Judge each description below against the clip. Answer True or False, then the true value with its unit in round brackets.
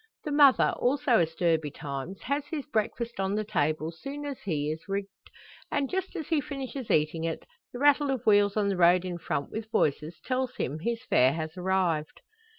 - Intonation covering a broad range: True (8.5 semitones)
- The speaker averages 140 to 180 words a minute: False (190 wpm)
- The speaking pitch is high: True (200 Hz)